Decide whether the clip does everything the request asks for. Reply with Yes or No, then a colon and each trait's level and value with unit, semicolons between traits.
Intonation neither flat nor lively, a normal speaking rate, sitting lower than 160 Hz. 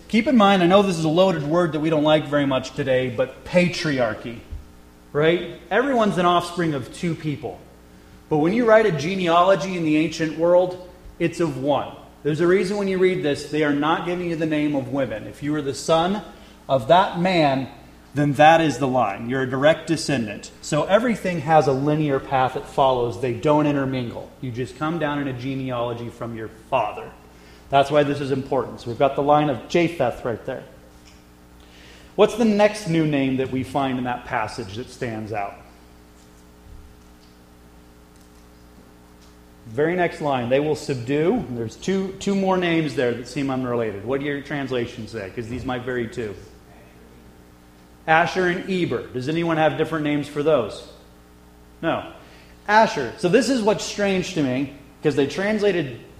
No: wide, 6.4 semitones; average, 180 wpm; medium, 140 Hz